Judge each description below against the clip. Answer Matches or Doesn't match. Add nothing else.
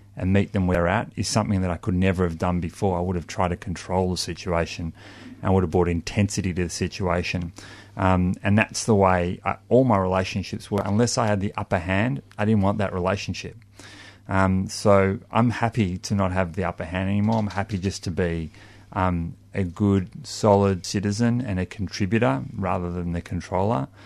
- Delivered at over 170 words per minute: Matches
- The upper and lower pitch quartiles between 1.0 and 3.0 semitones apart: Matches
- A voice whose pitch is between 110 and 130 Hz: Doesn't match